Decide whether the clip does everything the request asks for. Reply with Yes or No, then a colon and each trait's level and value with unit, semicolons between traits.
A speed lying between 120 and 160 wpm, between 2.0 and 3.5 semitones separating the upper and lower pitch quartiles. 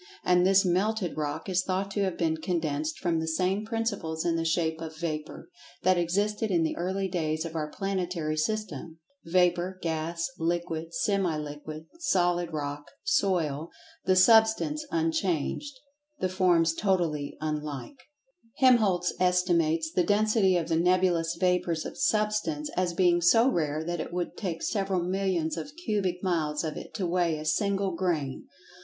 Yes: average, 155 wpm; average, 3.2 semitones